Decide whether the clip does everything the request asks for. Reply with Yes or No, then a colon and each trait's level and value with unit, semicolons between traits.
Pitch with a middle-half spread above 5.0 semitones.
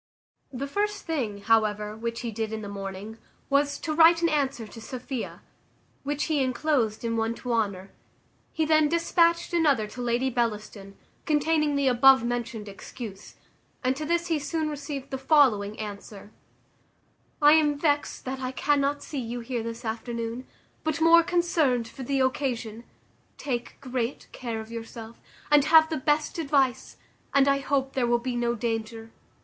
No: average, 4.5 semitones